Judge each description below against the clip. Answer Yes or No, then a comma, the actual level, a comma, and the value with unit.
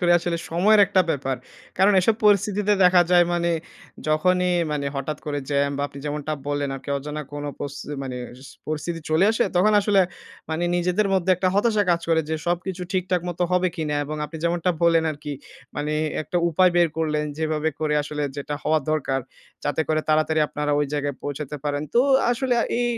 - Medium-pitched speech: Yes, medium, 160 Hz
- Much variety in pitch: No, average, 3.5 semitones